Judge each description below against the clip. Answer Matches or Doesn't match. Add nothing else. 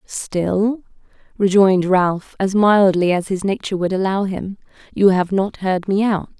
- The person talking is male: Doesn't match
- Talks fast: Doesn't match